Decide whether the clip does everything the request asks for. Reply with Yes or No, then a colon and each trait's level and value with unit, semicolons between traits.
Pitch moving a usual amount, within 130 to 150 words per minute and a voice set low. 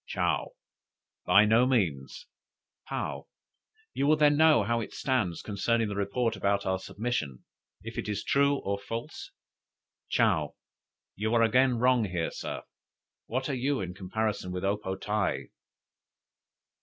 Yes: average, 4.3 semitones; average, 145 wpm; low, 110 Hz